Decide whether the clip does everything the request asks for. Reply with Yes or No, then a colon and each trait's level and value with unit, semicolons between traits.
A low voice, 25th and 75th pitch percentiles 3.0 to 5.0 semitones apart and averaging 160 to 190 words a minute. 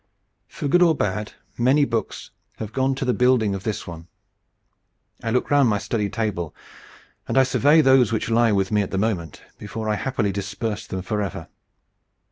Yes: low, 110 Hz; average, 4.2 semitones; average, 180 wpm